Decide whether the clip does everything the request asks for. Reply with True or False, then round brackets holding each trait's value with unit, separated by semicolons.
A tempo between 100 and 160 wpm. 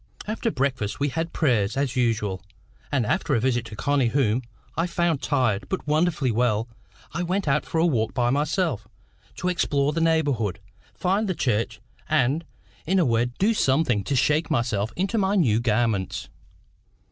False (170 wpm)